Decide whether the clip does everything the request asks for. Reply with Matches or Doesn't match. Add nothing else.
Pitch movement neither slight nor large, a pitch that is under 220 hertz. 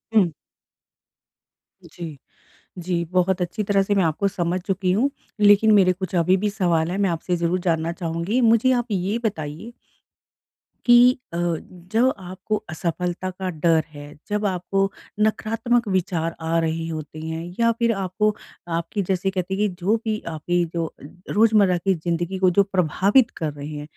Matches